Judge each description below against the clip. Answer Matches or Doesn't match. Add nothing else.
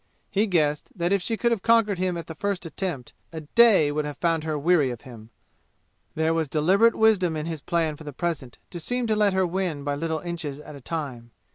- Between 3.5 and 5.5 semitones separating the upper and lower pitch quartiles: Matches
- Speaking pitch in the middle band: Matches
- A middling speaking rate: Doesn't match